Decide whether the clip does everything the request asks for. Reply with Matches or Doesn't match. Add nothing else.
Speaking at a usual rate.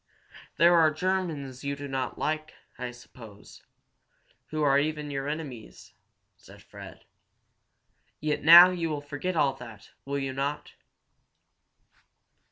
Doesn't match